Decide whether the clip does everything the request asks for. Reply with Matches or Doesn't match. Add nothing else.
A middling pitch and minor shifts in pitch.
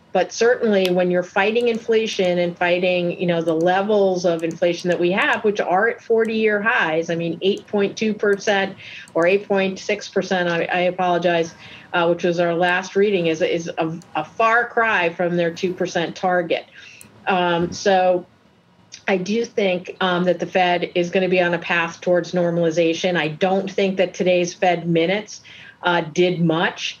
Matches